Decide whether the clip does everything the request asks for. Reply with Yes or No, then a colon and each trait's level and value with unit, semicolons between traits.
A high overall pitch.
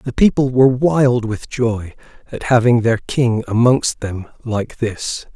No: low, 120 Hz